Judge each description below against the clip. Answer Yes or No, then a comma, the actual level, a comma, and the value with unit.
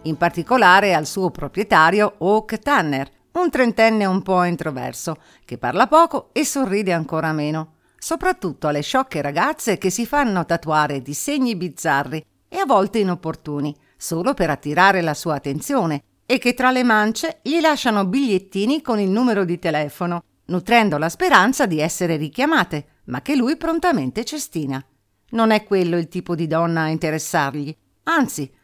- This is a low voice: No, medium, 185 Hz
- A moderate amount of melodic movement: No, wide, 7.6 semitones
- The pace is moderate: Yes, average, 155 wpm